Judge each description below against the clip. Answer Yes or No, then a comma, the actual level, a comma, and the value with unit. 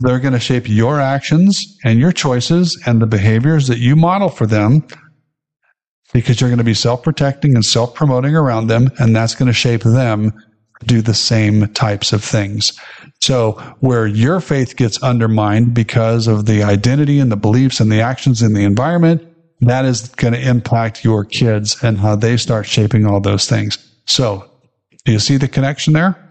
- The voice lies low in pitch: Yes, low, 120 Hz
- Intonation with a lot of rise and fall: No, average, 3.7 semitones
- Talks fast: No, average, 185 wpm